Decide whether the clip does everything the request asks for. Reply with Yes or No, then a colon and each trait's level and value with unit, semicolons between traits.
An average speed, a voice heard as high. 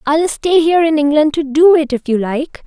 No: fast, 245 wpm; very high, 300 Hz